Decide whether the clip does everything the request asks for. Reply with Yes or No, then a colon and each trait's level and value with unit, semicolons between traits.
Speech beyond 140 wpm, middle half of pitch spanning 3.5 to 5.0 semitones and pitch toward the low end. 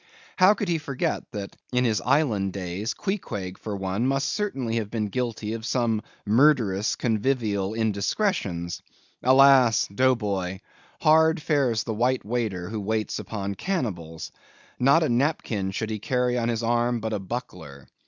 Yes: average, 155 wpm; average, 4.4 semitones; low, 115 Hz